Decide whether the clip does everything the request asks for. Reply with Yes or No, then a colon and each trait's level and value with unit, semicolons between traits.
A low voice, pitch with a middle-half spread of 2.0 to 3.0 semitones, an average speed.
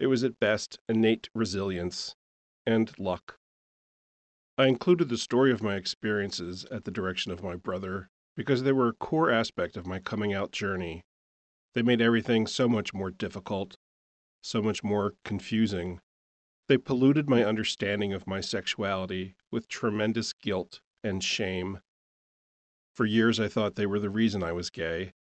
No: low, 100 Hz; average, 3.8 semitones; average, 155 wpm